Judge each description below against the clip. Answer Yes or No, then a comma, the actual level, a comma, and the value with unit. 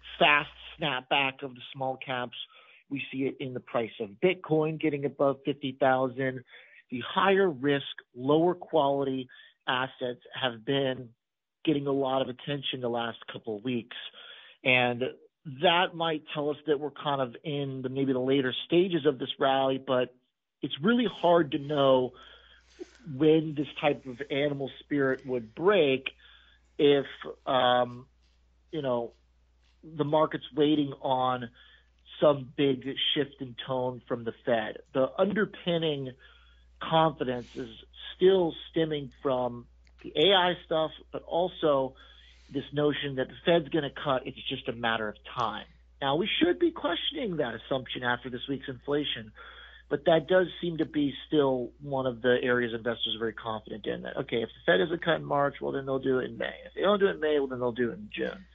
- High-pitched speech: No, low, 135 Hz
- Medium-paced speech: Yes, average, 170 wpm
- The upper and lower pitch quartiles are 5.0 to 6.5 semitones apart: No, average, 3.3 semitones